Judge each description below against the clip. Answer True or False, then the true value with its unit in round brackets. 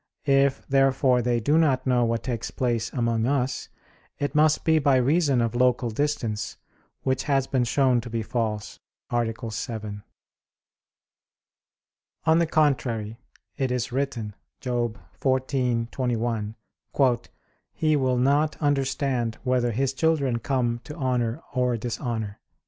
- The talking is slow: True (125 wpm)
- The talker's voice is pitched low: True (125 Hz)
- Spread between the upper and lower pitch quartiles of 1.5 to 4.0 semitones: True (2.8 semitones)